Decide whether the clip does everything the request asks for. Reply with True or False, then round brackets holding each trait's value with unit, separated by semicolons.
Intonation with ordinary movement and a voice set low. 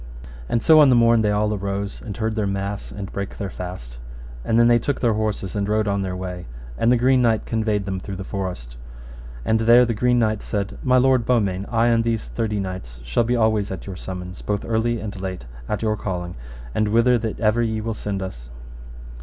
True (3.1 semitones; 105 Hz)